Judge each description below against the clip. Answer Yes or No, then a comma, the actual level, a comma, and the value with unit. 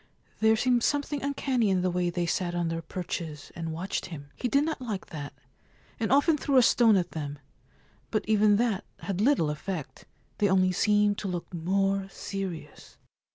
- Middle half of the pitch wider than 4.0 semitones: Yes, average, 4.7 semitones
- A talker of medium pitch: No, high, 195 Hz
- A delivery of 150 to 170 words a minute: No, average, 185 wpm